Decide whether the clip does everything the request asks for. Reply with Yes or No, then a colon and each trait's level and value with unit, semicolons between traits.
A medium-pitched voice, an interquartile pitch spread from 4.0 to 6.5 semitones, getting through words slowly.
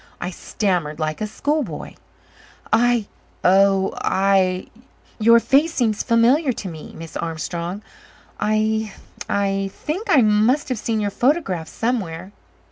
No: high, 210 Hz; average, 4.5 semitones; slow, 125 wpm